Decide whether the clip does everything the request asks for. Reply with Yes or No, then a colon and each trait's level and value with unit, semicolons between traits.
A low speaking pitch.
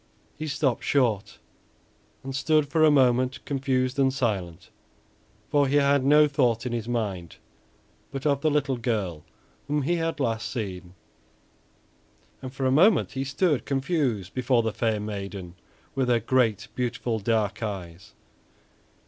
Yes: low, 130 Hz